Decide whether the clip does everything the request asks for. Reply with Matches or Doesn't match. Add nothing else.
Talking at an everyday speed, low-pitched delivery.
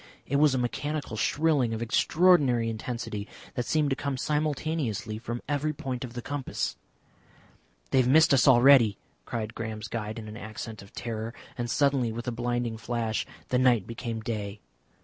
Matches